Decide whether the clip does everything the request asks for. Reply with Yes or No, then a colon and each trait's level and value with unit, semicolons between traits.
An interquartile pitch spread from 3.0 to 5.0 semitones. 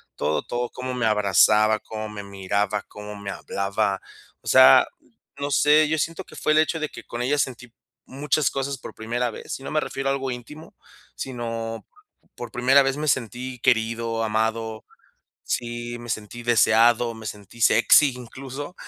Yes: average, 3.5 semitones